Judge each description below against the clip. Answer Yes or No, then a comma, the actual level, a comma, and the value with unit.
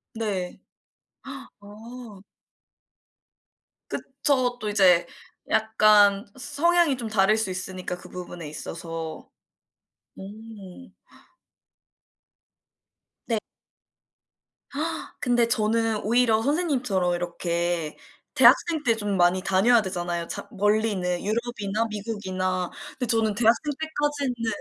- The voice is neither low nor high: No, high, 215 Hz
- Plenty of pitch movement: No, average, 4.4 semitones